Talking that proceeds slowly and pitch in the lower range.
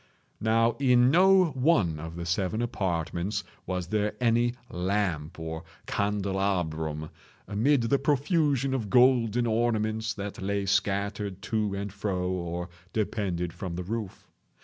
Yes: slow, 125 wpm; low, 100 Hz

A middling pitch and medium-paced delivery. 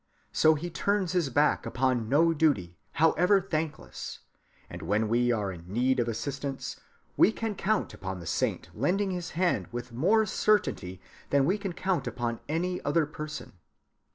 Yes: medium, 150 Hz; average, 160 wpm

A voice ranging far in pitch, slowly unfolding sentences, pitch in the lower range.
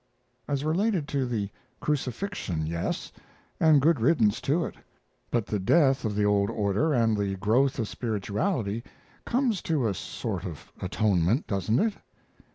No: wide, 6.8 semitones; average, 150 wpm; low, 120 Hz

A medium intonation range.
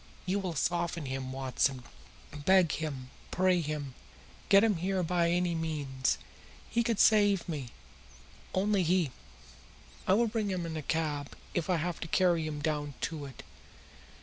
Yes: average, 4.1 semitones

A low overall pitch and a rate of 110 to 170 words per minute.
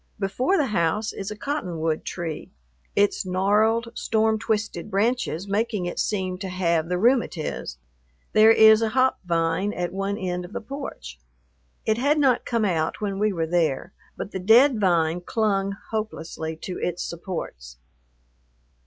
No: high, 195 Hz; average, 155 wpm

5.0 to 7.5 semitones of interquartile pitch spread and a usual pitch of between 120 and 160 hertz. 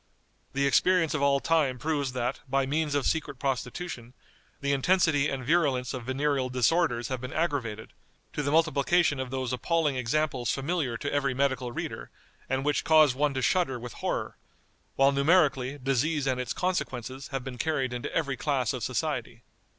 No: average, 3.1 semitones; low, 135 Hz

